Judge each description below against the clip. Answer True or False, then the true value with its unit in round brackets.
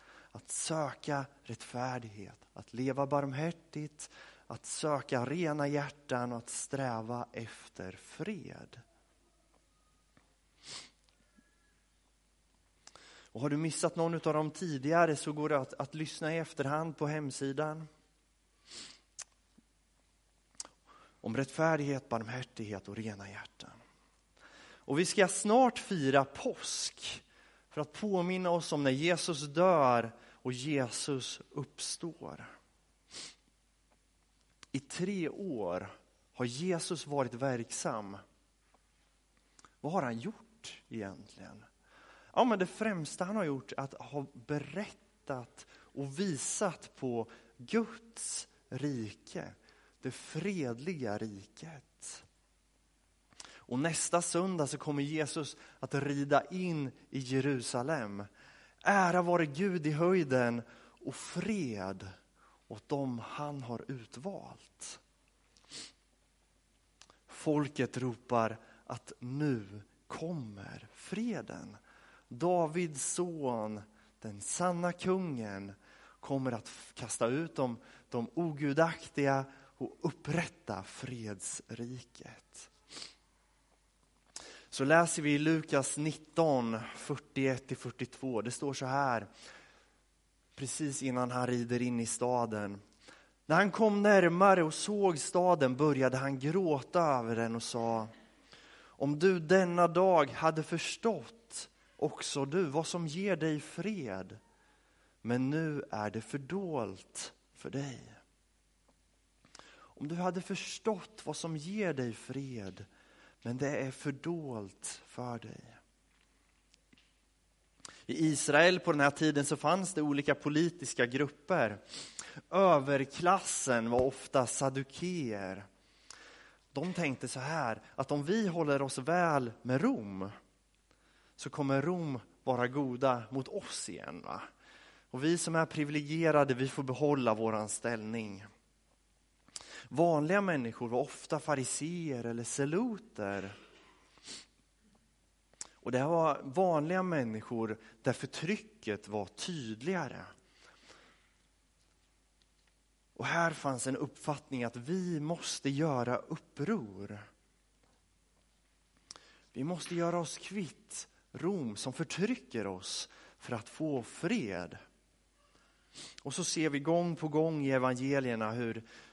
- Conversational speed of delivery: False (105 wpm)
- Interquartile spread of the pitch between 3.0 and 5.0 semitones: False (5.6 semitones)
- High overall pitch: False (140 Hz)